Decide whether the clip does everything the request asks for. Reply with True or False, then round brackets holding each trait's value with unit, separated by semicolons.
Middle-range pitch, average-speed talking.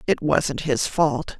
True (145 Hz; 170 wpm)